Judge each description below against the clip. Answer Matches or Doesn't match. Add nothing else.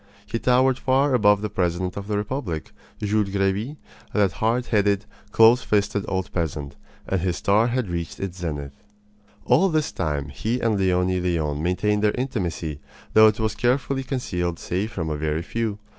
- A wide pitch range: Doesn't match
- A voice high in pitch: Doesn't match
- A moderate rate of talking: Matches